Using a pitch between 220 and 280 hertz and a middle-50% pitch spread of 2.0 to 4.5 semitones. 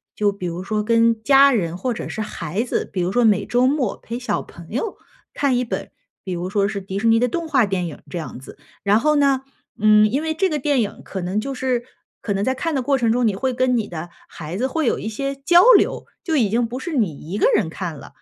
No: high, 230 Hz; average, 5.0 semitones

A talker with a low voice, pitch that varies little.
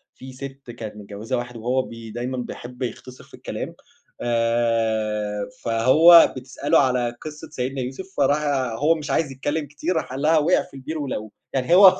No: low, 130 Hz; average, 4.0 semitones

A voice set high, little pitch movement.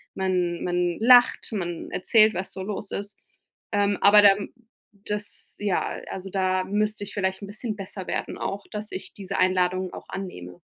Yes: high, 195 Hz; narrow, 1.9 semitones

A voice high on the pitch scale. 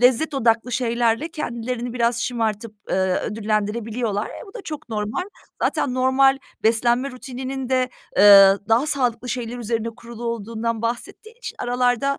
Yes: high, 235 Hz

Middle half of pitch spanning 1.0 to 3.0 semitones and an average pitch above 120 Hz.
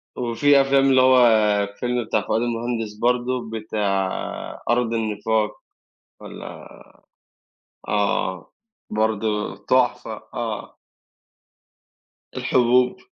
No: narrow, 2.5 semitones; low, 115 Hz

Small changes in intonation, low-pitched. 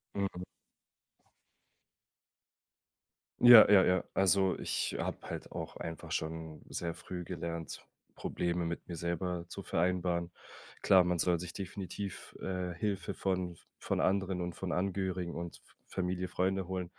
Yes: narrow, 1.7 semitones; very low, 90 Hz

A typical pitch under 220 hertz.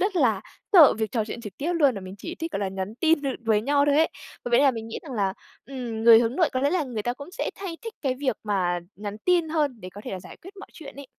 No: very high, 255 Hz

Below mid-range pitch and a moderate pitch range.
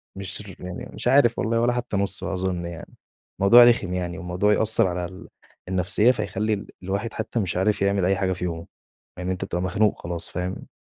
Yes: very low, 95 Hz; average, 3.1 semitones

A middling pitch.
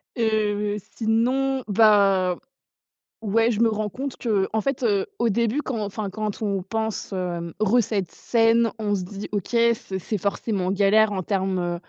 No: high, 210 Hz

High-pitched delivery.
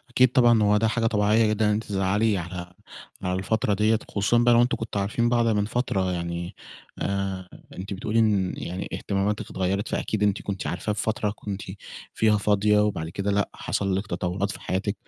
No: low, 105 Hz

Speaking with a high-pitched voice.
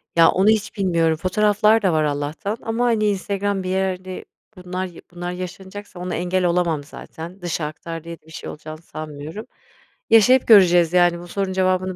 No: medium, 180 Hz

